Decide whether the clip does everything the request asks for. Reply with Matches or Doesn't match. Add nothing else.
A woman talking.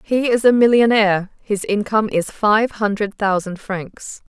Matches